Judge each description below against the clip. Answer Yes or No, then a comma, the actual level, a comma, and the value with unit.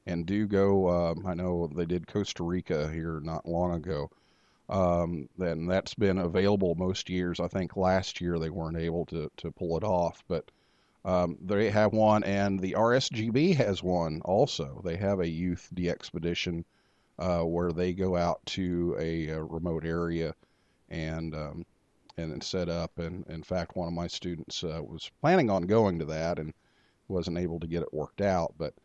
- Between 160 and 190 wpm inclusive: Yes, average, 185 wpm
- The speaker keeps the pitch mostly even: Yes, narrow, 2.0 semitones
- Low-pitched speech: Yes, very low, 85 Hz